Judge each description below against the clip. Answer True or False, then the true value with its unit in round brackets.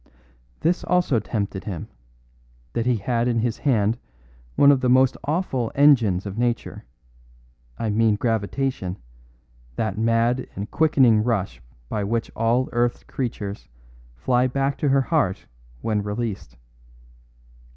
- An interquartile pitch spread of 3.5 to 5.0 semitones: True (3.9 semitones)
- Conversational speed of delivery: False (130 wpm)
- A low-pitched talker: True (115 Hz)